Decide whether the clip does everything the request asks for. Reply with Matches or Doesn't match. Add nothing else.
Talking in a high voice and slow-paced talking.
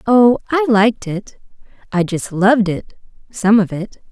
Matches